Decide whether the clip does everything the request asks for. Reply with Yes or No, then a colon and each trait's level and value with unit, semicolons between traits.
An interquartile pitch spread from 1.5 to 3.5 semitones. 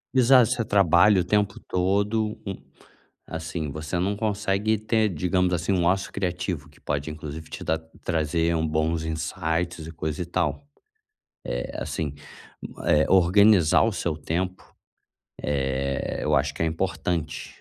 No: average, 4.2 semitones